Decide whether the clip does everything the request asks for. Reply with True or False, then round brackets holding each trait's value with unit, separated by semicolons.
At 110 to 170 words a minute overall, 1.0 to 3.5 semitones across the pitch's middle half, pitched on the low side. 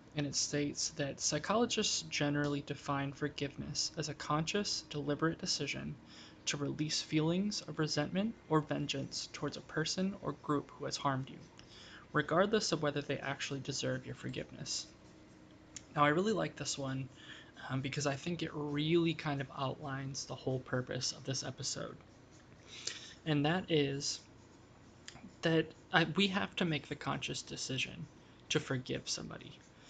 False (145 wpm; 2.7 semitones; 145 Hz)